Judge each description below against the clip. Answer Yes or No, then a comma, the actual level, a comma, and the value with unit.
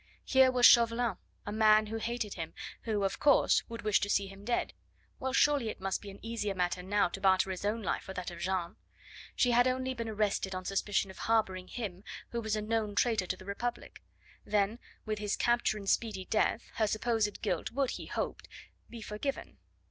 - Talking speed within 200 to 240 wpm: Yes, fast, 205 wpm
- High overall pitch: Yes, high, 215 Hz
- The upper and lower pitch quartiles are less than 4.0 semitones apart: Yes, average, 3.1 semitones